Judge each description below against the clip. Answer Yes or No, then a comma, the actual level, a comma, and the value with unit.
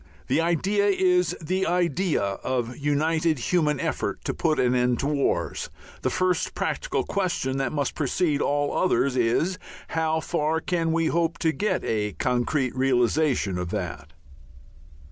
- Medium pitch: Yes, medium, 155 Hz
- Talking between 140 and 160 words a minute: Yes, average, 150 wpm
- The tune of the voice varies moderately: Yes, average, 5.0 semitones